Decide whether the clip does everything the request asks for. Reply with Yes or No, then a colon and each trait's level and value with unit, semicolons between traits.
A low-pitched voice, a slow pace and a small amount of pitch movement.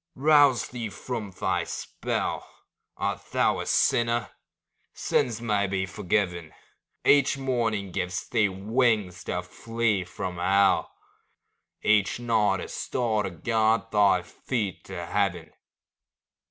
No: low, 105 Hz; slow, 115 wpm; average, 3.7 semitones